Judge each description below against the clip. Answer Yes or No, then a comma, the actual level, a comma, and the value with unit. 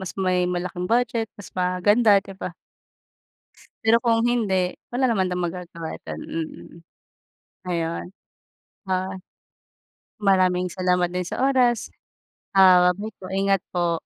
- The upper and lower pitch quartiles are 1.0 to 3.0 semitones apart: Yes, narrow, 2.5 semitones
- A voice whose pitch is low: No, medium, 185 Hz